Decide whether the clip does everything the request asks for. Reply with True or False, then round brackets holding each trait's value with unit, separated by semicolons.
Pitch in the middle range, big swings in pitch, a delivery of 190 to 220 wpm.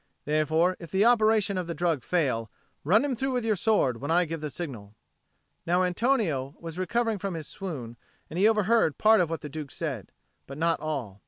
True (170 Hz; 5.9 semitones; 200 wpm)